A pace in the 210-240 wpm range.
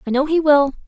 No: fast, 275 wpm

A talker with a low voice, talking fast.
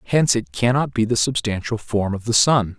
Yes: low, 115 Hz; fast, 215 wpm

